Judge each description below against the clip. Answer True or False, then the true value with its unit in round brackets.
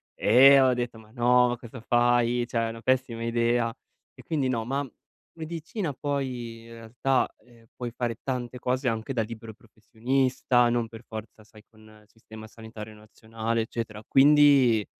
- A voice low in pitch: True (120 Hz)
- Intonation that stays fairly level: True (2.2 semitones)